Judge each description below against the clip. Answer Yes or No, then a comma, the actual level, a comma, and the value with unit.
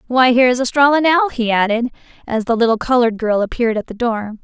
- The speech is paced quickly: Yes, fast, 215 wpm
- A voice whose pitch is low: No, high, 240 Hz